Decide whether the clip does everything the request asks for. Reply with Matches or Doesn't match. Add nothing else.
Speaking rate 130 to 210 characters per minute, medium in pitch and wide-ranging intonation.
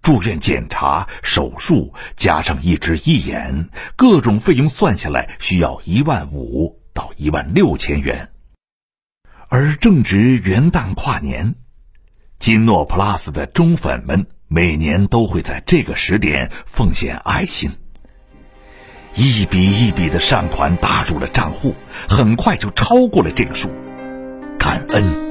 Doesn't match